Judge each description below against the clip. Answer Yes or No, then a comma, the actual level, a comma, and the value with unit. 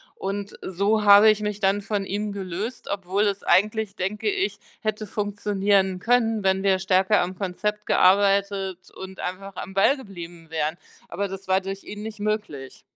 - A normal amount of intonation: No, narrow, 1.8 semitones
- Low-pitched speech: No, high, 200 Hz